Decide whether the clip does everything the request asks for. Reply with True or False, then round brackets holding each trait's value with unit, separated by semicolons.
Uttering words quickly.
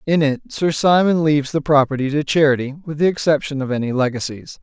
False (195 wpm)